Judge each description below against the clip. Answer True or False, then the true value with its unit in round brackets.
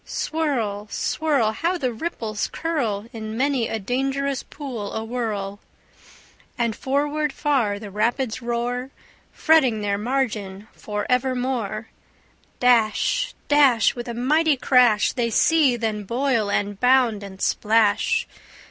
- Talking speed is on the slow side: True (120 wpm)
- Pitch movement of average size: True (4.2 semitones)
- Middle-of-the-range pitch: False (240 Hz)